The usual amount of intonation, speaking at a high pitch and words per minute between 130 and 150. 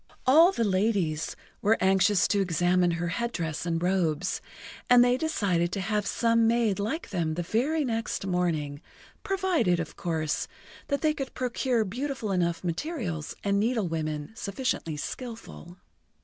No: wide, 5.9 semitones; high, 200 Hz; average, 145 wpm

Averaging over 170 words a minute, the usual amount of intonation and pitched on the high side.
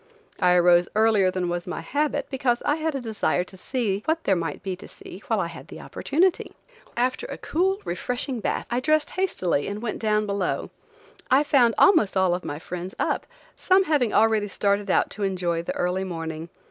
No: average, 195 wpm; wide, 6.4 semitones; high, 205 Hz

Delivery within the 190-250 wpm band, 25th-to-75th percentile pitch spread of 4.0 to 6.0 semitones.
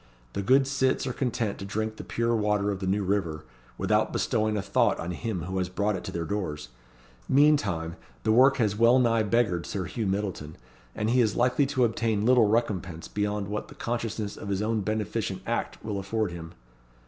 No: average, 200 wpm; average, 3.4 semitones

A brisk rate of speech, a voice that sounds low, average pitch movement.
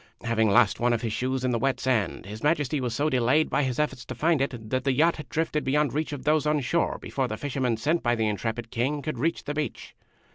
Yes: fast, 255 wpm; low, 130 Hz; average, 4.1 semitones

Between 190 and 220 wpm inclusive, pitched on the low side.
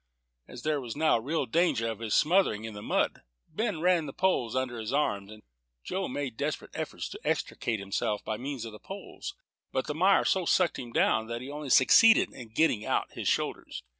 Yes: average, 200 wpm; low, 130 Hz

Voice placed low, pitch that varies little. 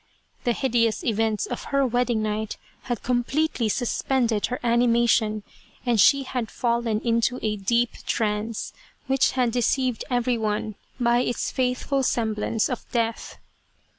No: high, 235 Hz; narrow, 2.2 semitones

